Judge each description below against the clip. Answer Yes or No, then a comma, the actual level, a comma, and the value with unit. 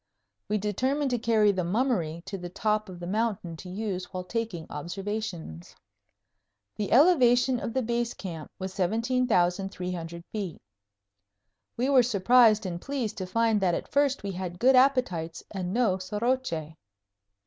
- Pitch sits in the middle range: No, high, 205 Hz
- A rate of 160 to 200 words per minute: No, average, 150 wpm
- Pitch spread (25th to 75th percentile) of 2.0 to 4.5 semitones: No, average, 5.0 semitones